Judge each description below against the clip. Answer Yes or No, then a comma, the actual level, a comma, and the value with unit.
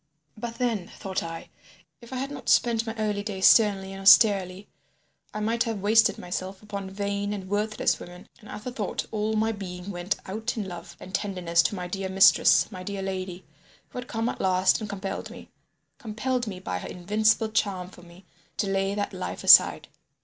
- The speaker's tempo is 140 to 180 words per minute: No, average, 190 wpm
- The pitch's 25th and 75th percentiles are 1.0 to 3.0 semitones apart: Yes, narrow, 2.6 semitones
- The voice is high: Yes, high, 200 Hz